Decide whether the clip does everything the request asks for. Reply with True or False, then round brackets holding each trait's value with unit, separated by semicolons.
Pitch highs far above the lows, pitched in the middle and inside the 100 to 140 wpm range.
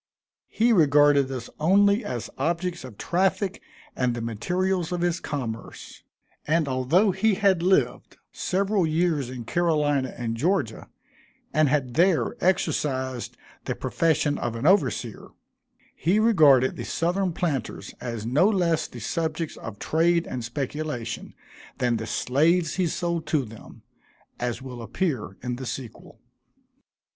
True (5.9 semitones; 155 Hz; 135 wpm)